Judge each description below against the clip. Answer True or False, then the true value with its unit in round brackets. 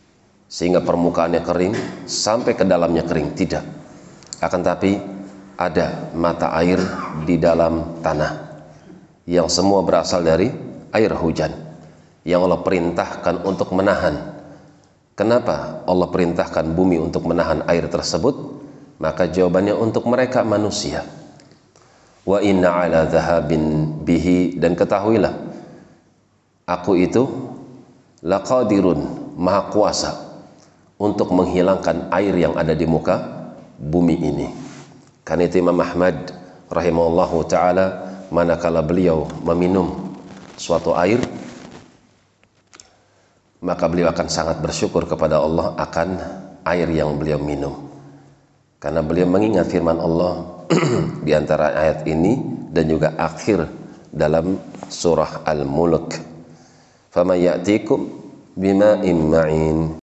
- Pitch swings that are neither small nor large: False (2.2 semitones)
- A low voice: True (85 Hz)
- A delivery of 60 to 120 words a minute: True (100 wpm)